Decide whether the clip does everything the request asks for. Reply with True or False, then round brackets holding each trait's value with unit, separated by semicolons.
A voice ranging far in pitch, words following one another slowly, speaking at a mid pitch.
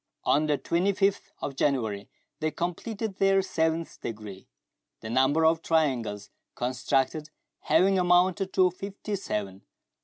True (6.5 semitones; 120 wpm; 160 Hz)